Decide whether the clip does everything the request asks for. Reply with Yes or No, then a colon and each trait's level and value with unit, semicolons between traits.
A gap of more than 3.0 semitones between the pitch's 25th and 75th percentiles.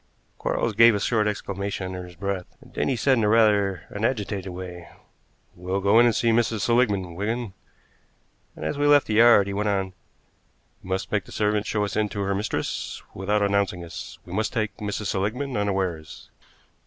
No: narrow, 2.6 semitones